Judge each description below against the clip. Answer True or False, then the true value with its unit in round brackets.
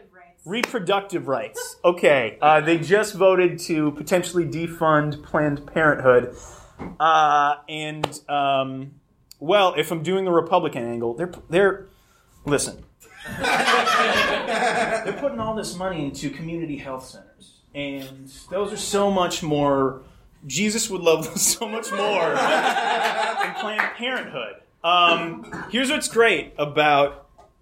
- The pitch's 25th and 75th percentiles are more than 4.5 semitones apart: True (5.2 semitones)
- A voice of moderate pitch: True (165 Hz)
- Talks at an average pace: False (120 wpm)